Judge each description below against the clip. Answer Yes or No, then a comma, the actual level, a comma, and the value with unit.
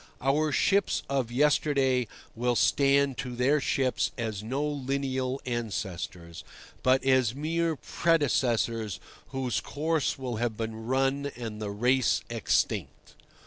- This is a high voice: No, low, 130 Hz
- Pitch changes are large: No, average, 3.3 semitones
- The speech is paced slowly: Yes, slow, 120 wpm